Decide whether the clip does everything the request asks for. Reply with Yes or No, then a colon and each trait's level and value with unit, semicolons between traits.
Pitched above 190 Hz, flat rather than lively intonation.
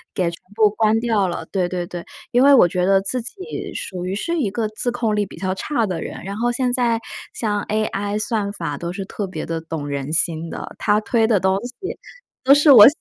No: high, 205 Hz; average, 4.3 semitones